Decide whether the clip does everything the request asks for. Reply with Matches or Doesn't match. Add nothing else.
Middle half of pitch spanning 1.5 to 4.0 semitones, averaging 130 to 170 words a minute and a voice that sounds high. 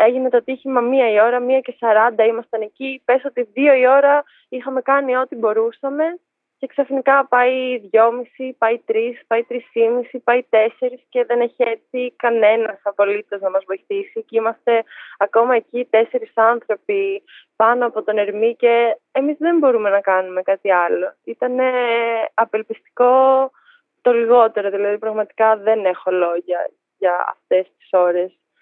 Matches